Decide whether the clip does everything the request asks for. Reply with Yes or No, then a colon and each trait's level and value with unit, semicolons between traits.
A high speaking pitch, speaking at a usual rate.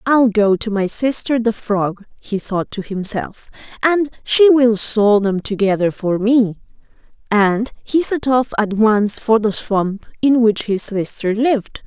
Yes: high, 220 Hz; average, 165 wpm